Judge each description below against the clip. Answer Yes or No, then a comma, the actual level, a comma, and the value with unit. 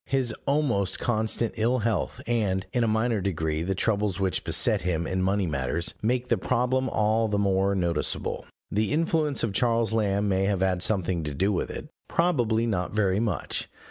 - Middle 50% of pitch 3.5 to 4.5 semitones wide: Yes, average, 3.8 semitones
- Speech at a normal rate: Yes, average, 180 wpm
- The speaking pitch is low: Yes, low, 105 Hz